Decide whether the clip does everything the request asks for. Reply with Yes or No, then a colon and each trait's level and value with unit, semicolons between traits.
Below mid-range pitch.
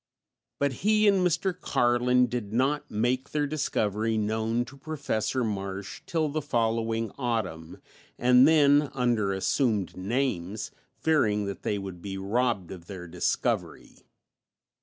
Yes: low, 115 Hz